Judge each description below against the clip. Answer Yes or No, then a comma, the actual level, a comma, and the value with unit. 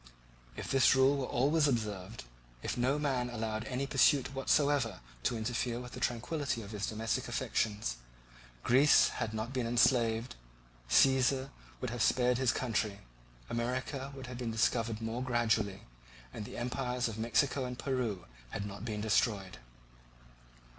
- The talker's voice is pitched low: Yes, low, 120 Hz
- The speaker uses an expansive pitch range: No, average, 2.9 semitones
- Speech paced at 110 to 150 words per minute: Yes, average, 145 wpm